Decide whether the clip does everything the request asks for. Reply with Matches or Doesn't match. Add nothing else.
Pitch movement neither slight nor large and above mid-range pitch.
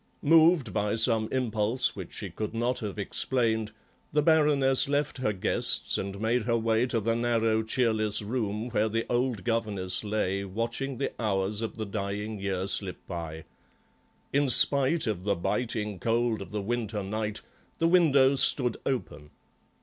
Doesn't match